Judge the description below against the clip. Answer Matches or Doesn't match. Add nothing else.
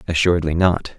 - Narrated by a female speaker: Doesn't match